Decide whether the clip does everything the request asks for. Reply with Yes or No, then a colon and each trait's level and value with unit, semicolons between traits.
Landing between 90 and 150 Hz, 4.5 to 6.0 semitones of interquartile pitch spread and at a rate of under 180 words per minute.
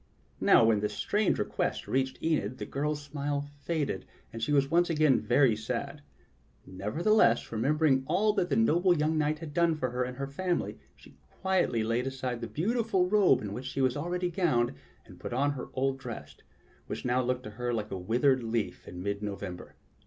No: low, 135 Hz; wide, 5.4 semitones; average, 190 wpm